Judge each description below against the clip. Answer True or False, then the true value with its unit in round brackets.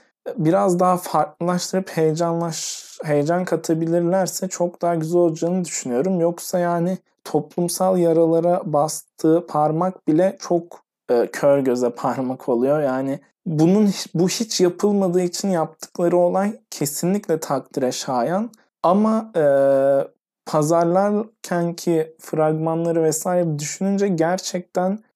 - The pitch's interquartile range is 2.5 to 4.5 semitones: True (2.8 semitones)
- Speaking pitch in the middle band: True (175 Hz)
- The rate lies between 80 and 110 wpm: True (100 wpm)